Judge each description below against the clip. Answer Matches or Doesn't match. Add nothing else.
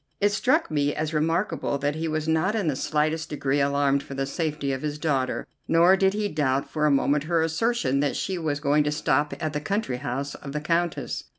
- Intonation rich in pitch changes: Doesn't match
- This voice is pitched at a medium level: Matches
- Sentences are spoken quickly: Matches